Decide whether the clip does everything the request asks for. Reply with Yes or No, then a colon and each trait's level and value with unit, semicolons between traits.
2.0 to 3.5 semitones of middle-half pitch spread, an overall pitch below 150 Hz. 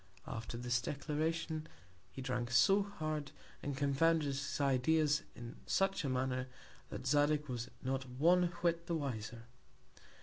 No: average, 3.9 semitones; medium, 140 Hz